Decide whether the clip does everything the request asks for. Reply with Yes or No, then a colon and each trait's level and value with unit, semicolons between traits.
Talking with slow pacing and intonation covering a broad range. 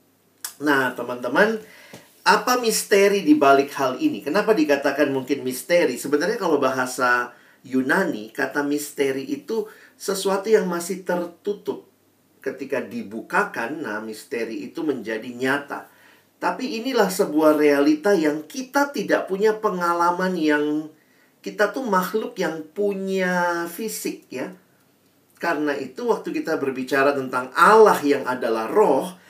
No: average, 115 wpm; wide, 7.0 semitones